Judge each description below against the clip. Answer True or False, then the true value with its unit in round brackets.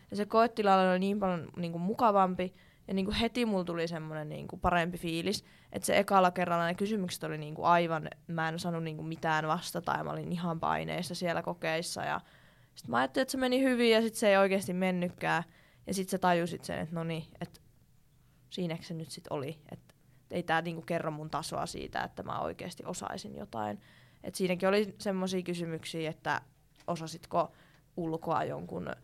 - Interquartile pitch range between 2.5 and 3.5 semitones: True (2.8 semitones)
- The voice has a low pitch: False (170 Hz)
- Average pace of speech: False (175 wpm)